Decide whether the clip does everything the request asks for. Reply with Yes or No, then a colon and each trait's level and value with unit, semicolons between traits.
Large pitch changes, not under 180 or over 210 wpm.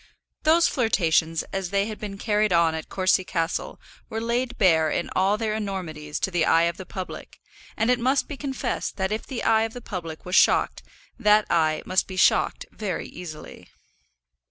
No: average, 4.7 semitones; average, 185 wpm